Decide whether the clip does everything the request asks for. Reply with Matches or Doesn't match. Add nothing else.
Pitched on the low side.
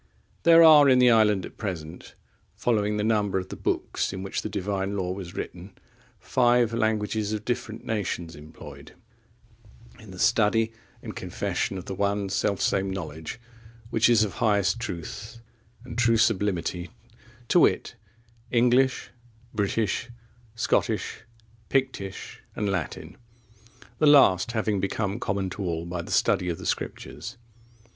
Matches